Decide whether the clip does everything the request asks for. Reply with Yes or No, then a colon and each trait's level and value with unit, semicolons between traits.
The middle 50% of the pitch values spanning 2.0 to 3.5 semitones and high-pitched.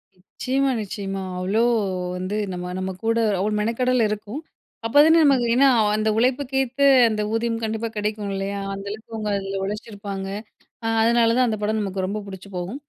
Yes: average, 3.1 semitones; high, 215 Hz